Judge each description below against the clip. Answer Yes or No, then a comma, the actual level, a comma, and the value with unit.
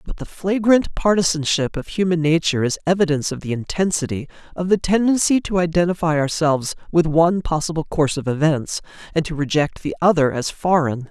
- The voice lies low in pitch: No, medium, 165 Hz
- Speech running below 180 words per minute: Yes, average, 165 wpm